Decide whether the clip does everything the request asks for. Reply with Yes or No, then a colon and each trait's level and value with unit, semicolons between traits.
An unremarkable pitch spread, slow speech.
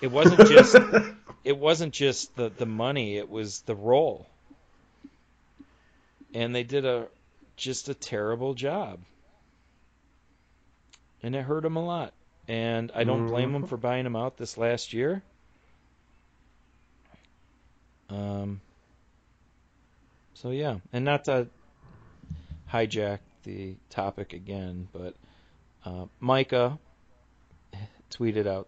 No: wide, 5.9 semitones; slow, 115 wpm